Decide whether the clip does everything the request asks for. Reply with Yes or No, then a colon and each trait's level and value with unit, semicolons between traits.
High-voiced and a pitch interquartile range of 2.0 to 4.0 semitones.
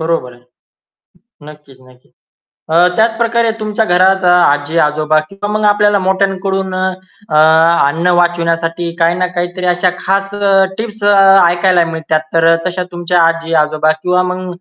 No: medium, 175 Hz; average, 2.8 semitones